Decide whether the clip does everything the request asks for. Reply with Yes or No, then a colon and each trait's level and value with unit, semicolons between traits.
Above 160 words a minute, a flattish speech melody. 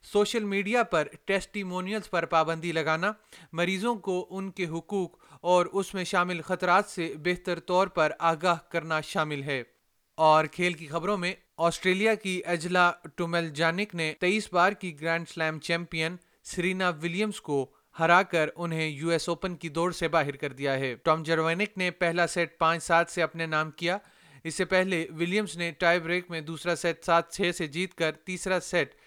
Yes: average, 180 wpm; narrow, 2.2 semitones